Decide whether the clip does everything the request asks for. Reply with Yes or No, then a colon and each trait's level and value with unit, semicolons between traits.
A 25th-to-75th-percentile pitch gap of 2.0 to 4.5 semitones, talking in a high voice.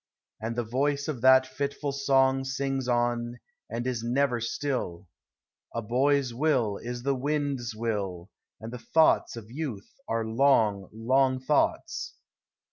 No: average, 3.1 semitones; low, 125 Hz